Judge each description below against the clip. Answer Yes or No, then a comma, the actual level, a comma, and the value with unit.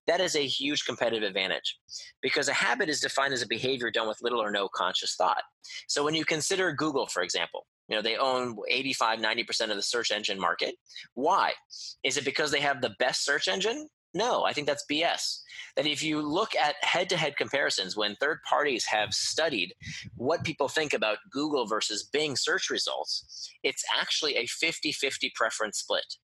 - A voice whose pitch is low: No, medium, 145 Hz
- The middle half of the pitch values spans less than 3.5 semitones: No, average, 4.0 semitones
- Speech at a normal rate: Yes, average, 190 wpm